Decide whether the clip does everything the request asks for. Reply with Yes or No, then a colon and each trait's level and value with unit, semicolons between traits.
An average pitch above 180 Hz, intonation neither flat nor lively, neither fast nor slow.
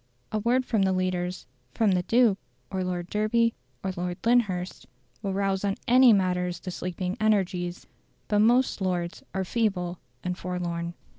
Yes: high, 190 Hz; average, 3.1 semitones; average, 155 wpm